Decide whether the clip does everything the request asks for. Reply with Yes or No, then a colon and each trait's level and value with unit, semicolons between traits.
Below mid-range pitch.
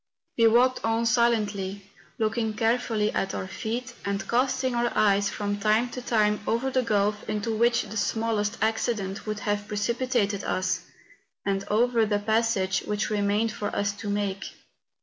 No: high, 215 Hz